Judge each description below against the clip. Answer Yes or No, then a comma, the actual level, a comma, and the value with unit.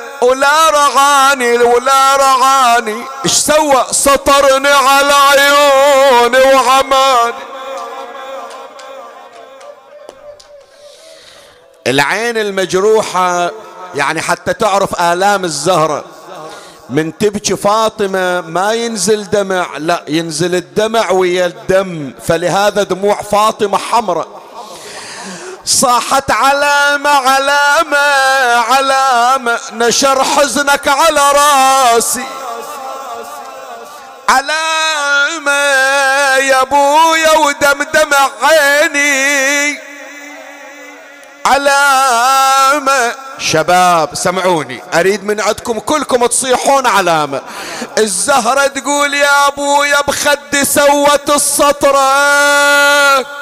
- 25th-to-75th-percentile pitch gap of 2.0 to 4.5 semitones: No, average, 5.2 semitones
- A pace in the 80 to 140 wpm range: No, average, 70 wpm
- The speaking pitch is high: Yes, very high, 270 Hz